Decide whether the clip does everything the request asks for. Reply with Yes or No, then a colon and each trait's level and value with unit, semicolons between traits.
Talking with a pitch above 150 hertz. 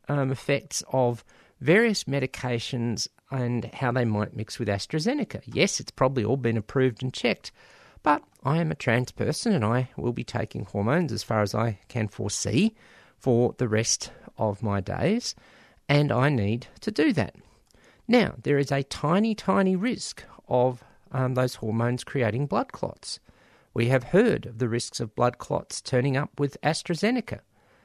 No: low, 125 Hz